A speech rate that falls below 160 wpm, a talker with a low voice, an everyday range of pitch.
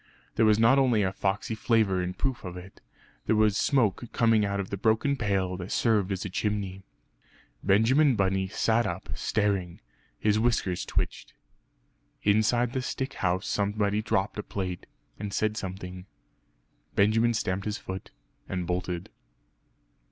Yes: average, 150 wpm; low, 105 Hz; average, 3.0 semitones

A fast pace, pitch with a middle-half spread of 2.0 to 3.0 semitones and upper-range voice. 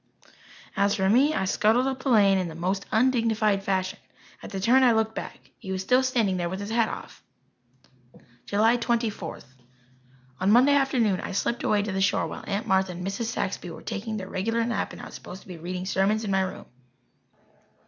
No: fast, 210 wpm; average, 3.5 semitones; high, 205 Hz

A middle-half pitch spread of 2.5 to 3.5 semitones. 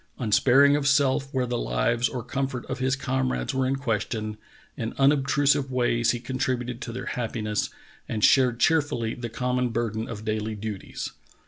Yes: average, 2.9 semitones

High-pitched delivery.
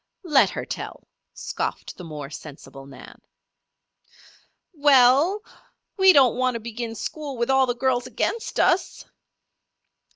Yes: very high, 255 Hz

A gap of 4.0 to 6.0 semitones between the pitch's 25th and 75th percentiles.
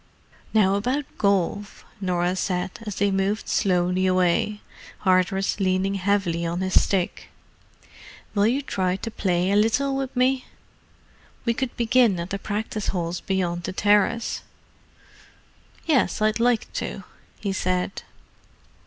No: average, 3.1 semitones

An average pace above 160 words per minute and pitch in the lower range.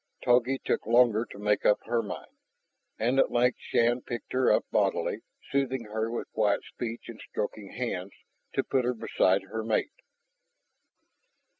No: average, 155 wpm; low, 115 Hz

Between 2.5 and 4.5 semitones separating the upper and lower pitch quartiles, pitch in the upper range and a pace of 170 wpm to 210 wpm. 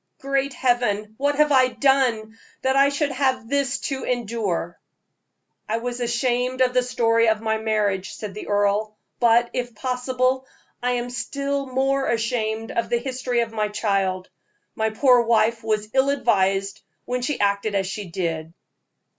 No: average, 3.3 semitones; high, 235 Hz; average, 160 wpm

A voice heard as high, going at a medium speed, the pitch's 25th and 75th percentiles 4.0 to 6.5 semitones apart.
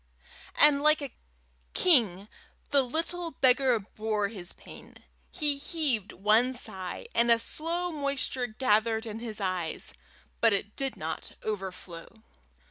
No: high, 235 Hz; slow, 125 wpm; average, 5.2 semitones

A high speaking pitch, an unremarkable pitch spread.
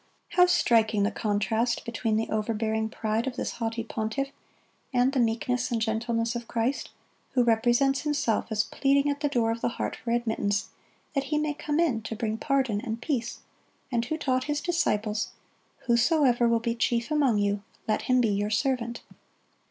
Yes: high, 235 Hz; average, 3.5 semitones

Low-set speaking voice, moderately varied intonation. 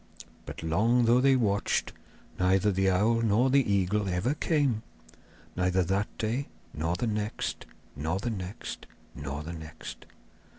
Yes: low, 100 Hz; average, 4.4 semitones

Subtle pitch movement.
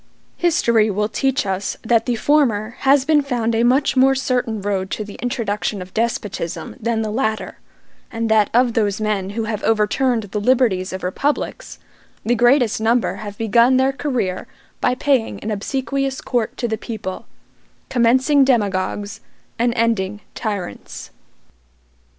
No: average, 3.5 semitones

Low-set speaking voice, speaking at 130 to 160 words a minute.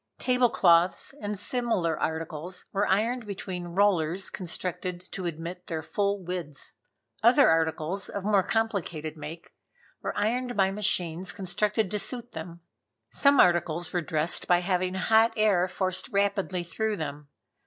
No: medium, 185 Hz; average, 140 wpm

